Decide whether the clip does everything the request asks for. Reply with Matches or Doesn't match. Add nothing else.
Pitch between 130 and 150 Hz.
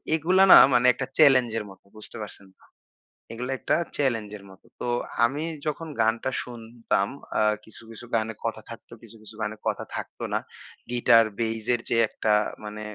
Doesn't match